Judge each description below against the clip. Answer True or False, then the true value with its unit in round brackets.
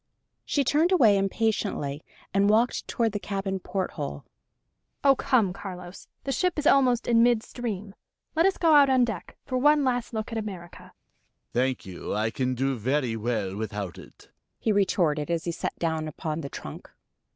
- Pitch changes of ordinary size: False (8.7 semitones)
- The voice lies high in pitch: True (195 Hz)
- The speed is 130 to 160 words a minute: False (175 wpm)